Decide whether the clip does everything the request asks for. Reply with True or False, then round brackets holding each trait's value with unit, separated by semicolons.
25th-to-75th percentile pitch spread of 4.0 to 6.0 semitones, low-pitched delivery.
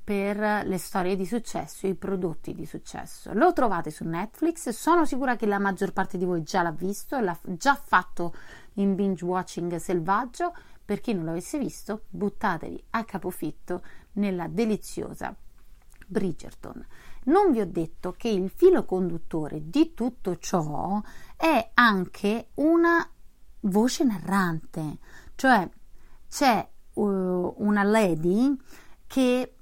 False (4.9 semitones; 200 Hz)